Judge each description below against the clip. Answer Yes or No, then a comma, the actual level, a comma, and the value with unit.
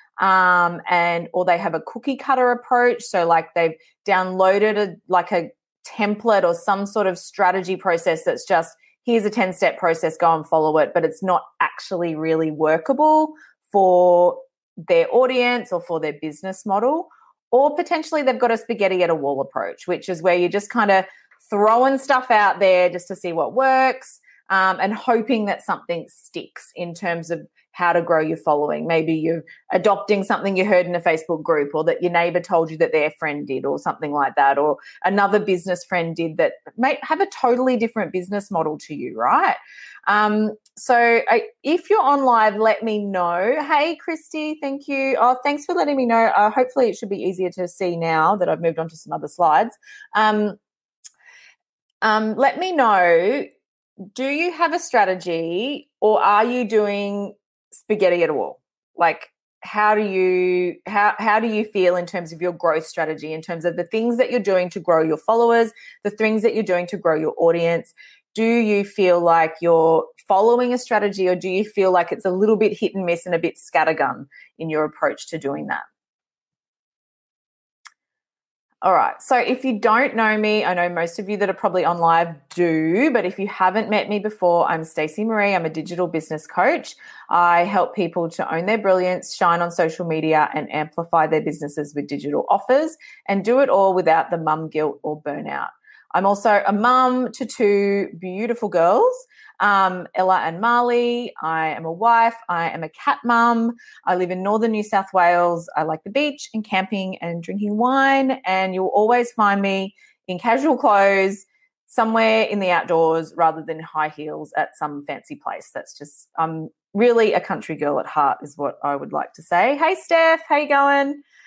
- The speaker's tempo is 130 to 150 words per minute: No, average, 190 wpm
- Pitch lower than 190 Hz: No, high, 195 Hz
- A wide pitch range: Yes, wide, 5.7 semitones